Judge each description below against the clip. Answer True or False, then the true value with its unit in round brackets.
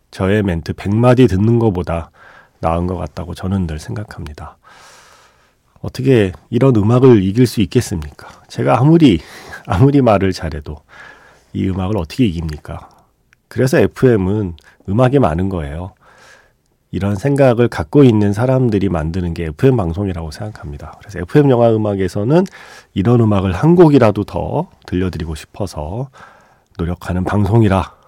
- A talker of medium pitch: False (100 Hz)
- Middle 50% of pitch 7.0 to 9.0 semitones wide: False (5.5 semitones)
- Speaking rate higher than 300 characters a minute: True (315 characters per minute)